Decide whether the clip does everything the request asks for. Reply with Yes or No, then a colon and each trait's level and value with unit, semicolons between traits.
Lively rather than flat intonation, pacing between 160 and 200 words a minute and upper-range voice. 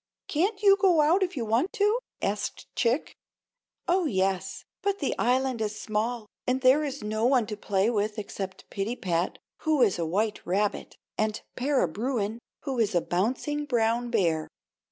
Yes: wide, 5.9 semitones; average, 165 wpm; high, 230 Hz